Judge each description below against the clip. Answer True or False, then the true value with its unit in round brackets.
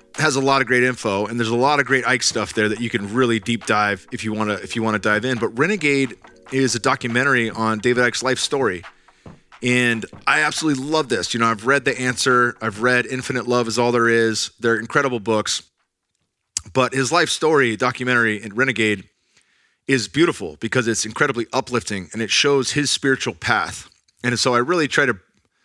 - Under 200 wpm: False (205 wpm)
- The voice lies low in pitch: True (120 Hz)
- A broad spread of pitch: False (2.7 semitones)